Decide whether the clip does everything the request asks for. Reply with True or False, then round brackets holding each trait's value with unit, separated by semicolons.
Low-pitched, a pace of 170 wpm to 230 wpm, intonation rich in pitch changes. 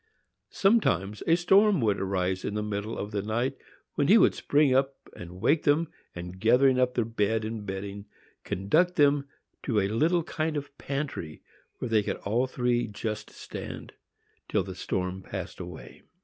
True (115 Hz; 175 wpm; 6.1 semitones)